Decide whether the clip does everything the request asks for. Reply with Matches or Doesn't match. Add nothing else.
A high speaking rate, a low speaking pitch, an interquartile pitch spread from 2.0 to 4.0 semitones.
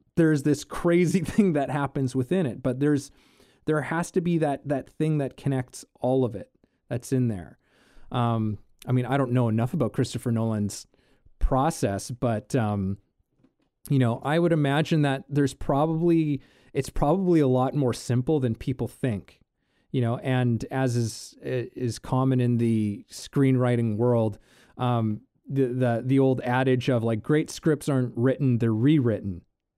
Doesn't match